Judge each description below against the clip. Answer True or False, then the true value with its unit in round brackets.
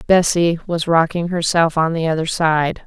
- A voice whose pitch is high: False (165 Hz)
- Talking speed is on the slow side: False (170 wpm)